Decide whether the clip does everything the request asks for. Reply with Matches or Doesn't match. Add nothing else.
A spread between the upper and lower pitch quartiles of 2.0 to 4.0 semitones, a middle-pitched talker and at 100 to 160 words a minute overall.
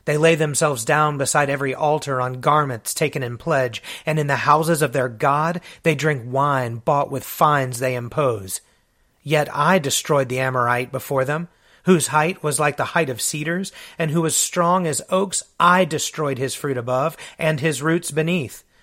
Doesn't match